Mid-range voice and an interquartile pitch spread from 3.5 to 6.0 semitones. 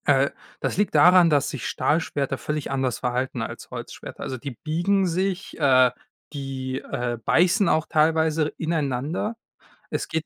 Yes: medium, 150 Hz; average, 3.9 semitones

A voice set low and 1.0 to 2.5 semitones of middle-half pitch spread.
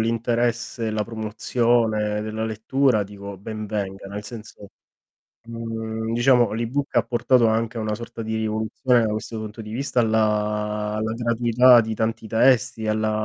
Yes: low, 110 Hz; narrow, 1.6 semitones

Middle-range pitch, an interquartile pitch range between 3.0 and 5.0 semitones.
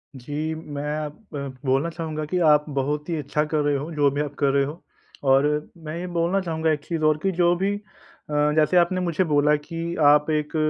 No: medium, 150 Hz; narrow, 2.4 semitones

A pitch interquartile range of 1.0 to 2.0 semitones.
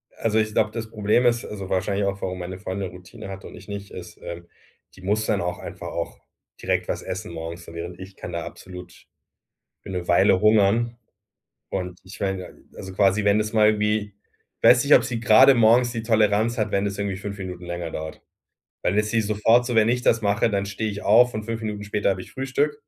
No: average, 2.9 semitones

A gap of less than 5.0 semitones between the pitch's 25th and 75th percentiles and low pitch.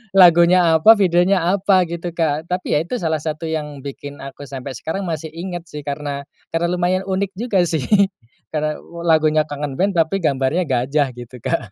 No: average, 3.6 semitones; medium, 160 Hz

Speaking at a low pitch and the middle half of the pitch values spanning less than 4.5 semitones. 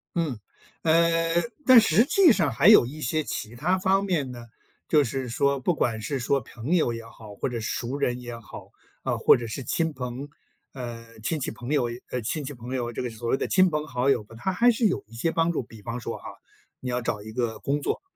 No: low, 130 Hz; wide, 5.5 semitones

